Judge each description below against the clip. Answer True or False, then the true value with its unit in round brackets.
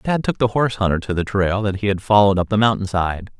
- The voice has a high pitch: False (100 Hz)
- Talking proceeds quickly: True (285 wpm)